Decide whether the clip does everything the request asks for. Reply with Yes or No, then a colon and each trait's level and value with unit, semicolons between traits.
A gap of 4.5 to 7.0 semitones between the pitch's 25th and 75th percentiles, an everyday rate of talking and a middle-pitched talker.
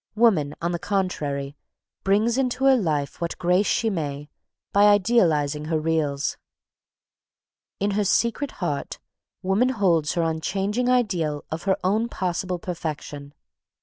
No: average, 5.3 semitones; slow, 130 wpm; medium, 180 Hz